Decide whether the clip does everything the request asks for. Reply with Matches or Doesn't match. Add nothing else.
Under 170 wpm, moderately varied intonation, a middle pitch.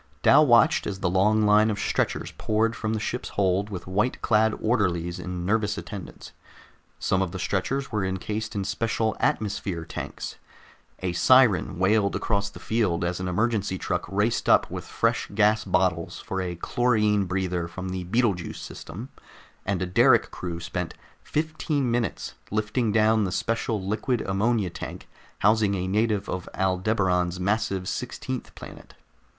Doesn't match